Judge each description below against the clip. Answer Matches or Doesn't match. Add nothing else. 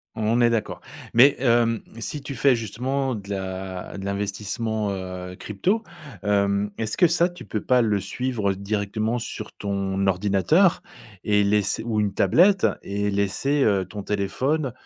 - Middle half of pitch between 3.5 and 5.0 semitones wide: Matches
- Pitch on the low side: Matches